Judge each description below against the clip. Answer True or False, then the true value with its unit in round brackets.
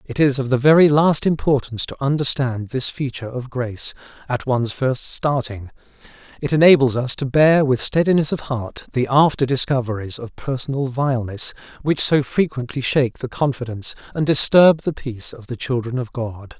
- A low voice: True (130 Hz)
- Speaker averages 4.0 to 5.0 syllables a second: False (5.3 syllables/s)